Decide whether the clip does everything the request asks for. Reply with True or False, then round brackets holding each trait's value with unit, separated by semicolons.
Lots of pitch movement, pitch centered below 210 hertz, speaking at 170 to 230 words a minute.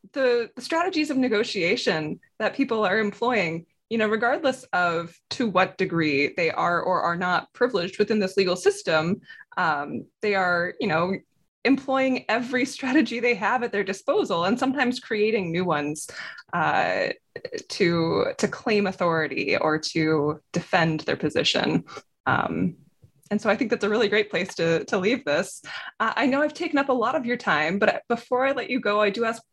False (6.2 semitones; 215 Hz; 180 wpm)